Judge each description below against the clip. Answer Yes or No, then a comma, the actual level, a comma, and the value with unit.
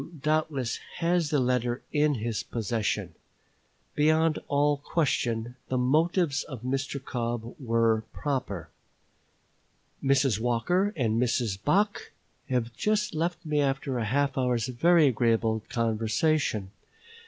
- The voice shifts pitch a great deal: No, average, 4.8 semitones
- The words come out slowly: Yes, slow, 120 wpm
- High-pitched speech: No, low, 130 Hz